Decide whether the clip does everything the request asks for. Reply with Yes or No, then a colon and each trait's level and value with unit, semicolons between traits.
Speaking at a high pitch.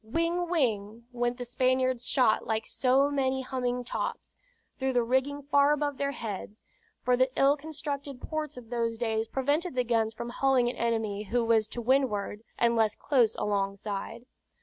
Yes: high, 245 Hz